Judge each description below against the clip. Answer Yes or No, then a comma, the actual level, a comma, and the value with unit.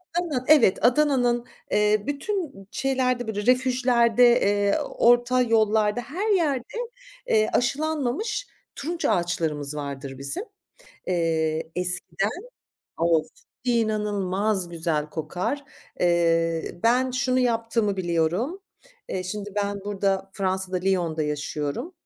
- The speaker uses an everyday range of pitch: No, wide, 6.4 semitones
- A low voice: No, high, 210 Hz